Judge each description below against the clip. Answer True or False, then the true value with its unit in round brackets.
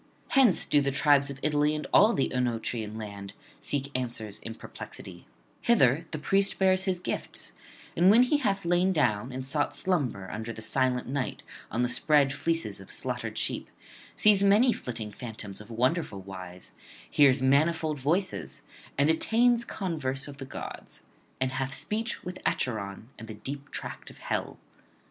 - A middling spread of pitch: False (6.7 semitones)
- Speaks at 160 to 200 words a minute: True (165 wpm)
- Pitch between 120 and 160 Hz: True (140 Hz)